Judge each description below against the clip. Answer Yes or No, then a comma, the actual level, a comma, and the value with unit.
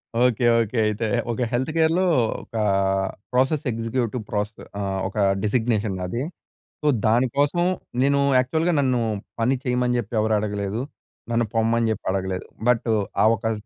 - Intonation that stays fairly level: No, average, 3.0 semitones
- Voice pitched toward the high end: No, low, 115 Hz